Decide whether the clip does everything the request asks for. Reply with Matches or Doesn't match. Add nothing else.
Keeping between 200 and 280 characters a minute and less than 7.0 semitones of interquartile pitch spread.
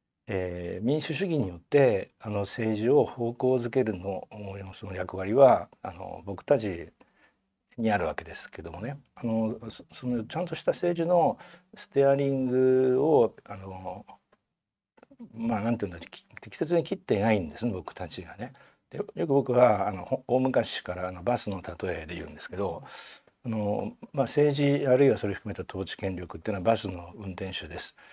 Doesn't match